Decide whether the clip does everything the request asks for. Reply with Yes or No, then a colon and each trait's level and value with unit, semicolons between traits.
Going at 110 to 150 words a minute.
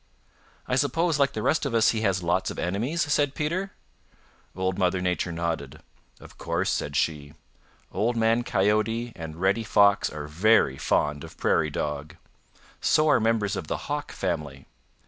No: average, 165 wpm